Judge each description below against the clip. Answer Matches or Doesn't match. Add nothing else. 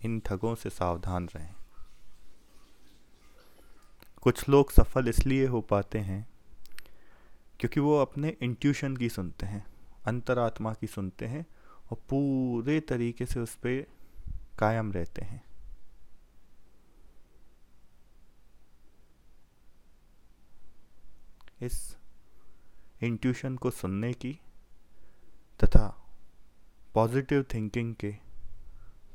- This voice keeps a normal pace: Doesn't match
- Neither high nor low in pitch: Doesn't match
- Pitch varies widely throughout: Doesn't match